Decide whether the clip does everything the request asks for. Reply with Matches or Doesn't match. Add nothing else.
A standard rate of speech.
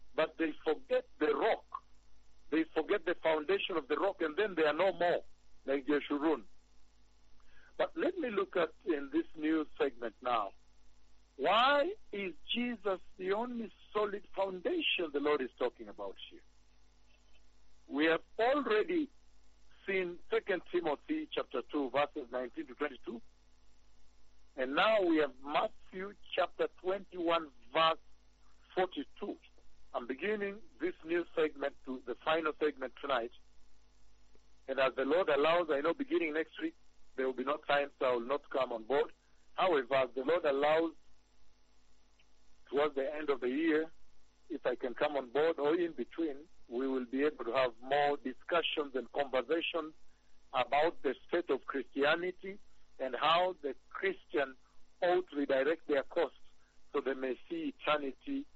Matches